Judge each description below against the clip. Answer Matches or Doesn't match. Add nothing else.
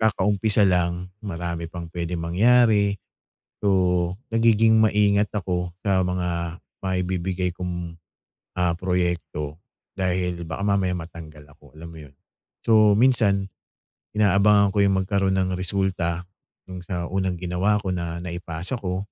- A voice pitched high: Doesn't match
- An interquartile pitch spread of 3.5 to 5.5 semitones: Doesn't match